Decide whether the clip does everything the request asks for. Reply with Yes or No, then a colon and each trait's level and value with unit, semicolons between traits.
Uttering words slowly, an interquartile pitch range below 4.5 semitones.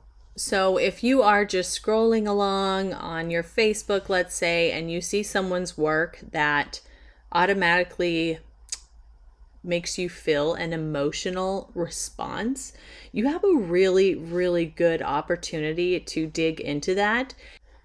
Yes: slow, 120 wpm; average, 3.3 semitones